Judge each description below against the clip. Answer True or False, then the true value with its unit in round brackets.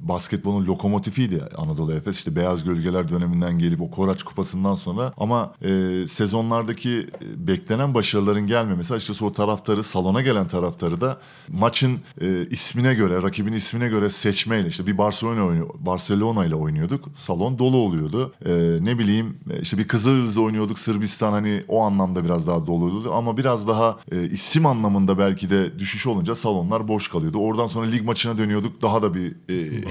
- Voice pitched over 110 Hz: False (105 Hz)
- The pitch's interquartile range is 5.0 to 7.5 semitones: False (3.9 semitones)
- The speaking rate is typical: False (160 wpm)